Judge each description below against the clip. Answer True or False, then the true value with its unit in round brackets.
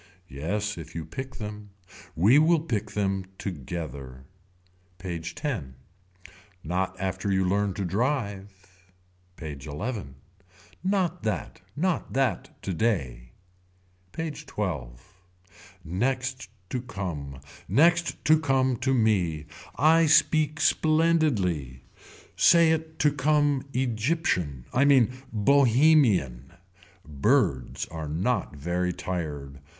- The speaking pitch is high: False (105 Hz)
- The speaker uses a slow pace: True (105 wpm)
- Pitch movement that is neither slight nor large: False (8.9 semitones)